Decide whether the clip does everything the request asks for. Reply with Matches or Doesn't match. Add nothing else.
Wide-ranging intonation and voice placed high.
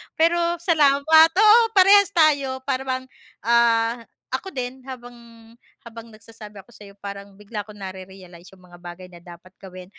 Matches